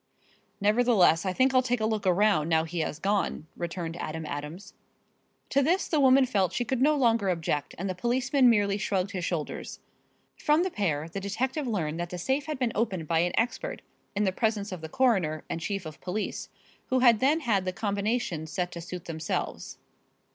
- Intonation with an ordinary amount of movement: No, wide, 6.2 semitones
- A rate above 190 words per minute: Yes, average, 200 wpm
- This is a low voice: No, high, 200 Hz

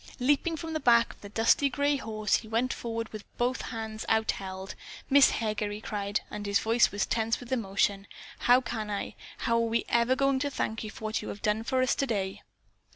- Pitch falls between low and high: No, high, 225 Hz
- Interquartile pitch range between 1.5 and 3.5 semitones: Yes, average, 3.2 semitones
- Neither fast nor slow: No, fast, 215 wpm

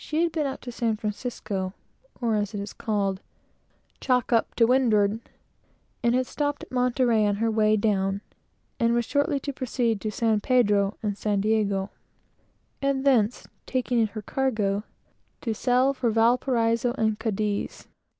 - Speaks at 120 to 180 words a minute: Yes, average, 155 wpm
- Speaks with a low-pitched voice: No, high, 225 Hz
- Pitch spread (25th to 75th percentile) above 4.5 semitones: No, average, 3.3 semitones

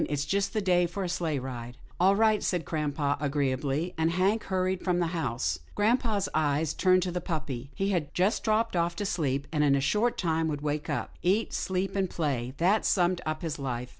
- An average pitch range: Yes, average, 4.7 semitones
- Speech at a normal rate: No, fast, 210 wpm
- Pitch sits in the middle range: Yes, medium, 170 Hz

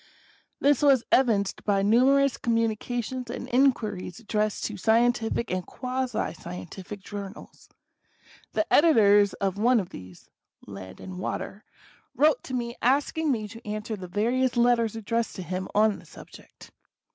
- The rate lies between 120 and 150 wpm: Yes, average, 140 wpm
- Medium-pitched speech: No, high, 225 Hz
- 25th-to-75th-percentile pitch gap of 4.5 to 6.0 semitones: No, average, 3.6 semitones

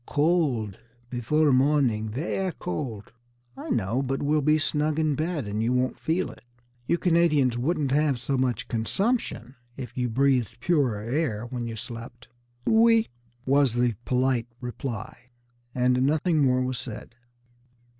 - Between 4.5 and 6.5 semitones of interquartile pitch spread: No, average, 4.1 semitones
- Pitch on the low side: Yes, low, 130 Hz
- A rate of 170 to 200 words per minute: No, average, 145 wpm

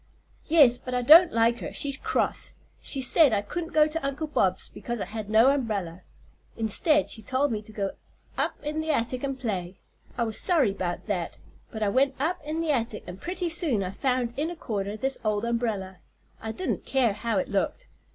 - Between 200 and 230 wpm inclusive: Yes, fast, 205 wpm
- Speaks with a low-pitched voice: No, high, 240 Hz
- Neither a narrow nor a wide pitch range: No, wide, 5.8 semitones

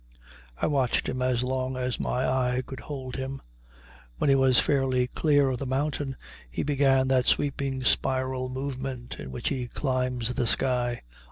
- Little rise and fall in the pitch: Yes, narrow, 1.1 semitones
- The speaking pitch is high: No, low, 130 Hz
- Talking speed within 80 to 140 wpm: No, average, 165 wpm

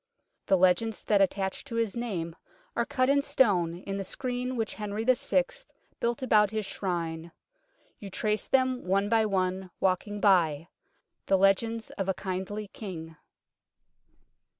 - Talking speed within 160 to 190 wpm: No, average, 150 wpm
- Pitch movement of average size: Yes, average, 3.7 semitones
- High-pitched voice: Yes, high, 200 Hz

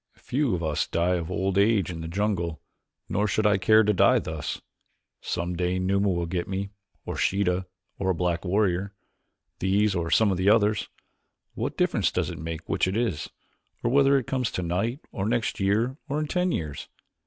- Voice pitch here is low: Yes, very low, 95 Hz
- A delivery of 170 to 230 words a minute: Yes, average, 190 wpm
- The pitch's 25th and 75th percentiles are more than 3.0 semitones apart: Yes, average, 3.7 semitones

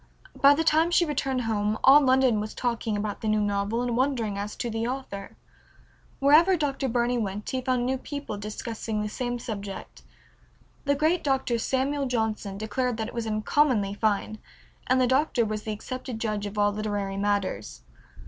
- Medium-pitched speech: No, high, 230 Hz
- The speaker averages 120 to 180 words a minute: Yes, average, 175 wpm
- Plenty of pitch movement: No, average, 3.9 semitones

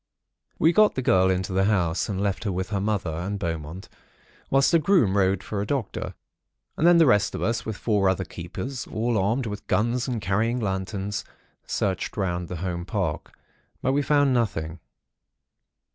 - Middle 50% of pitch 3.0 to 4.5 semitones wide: Yes, average, 4.2 semitones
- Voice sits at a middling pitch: No, low, 100 Hz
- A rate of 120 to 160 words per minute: No, average, 180 wpm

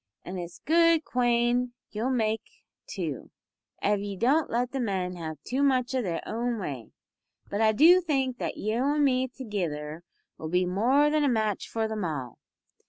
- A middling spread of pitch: No, wide, 5.8 semitones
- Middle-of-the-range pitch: No, high, 230 Hz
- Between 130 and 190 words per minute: Yes, average, 175 wpm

